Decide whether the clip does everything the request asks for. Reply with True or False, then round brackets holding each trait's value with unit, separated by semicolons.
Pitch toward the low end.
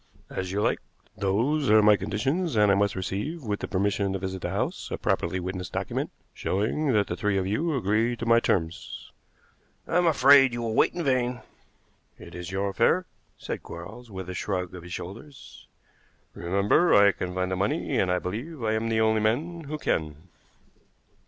True (105 Hz)